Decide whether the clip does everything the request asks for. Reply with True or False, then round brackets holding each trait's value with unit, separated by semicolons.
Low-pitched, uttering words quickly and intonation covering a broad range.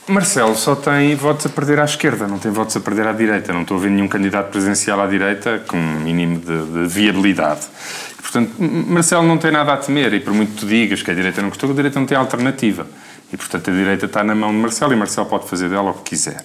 True (105 Hz; 260 wpm; 6.5 semitones)